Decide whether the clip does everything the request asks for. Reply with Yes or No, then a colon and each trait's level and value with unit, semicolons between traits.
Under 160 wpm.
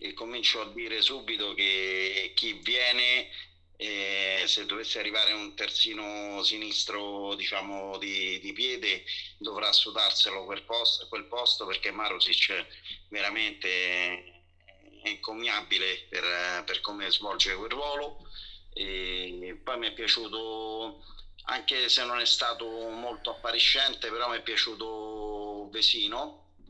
Yes: slow, 115 wpm